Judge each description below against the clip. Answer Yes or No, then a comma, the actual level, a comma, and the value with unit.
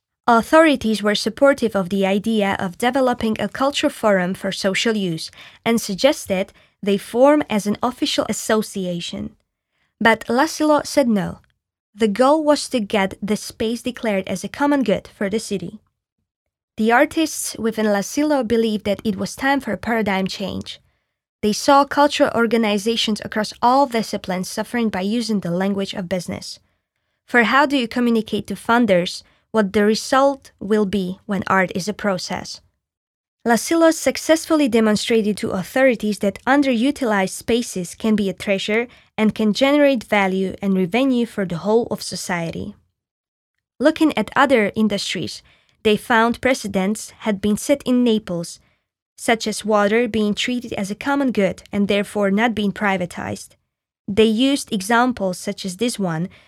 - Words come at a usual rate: Yes, average, 150 wpm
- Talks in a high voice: Yes, high, 220 Hz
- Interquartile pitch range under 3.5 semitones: No, average, 3.8 semitones